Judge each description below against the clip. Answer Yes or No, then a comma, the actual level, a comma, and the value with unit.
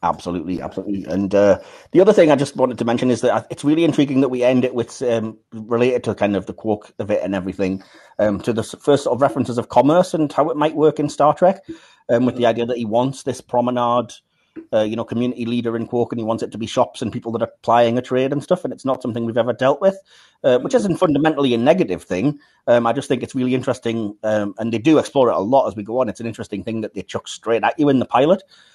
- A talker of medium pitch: No, low, 120 Hz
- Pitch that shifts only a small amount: No, average, 3.6 semitones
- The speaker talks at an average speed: No, fast, 270 wpm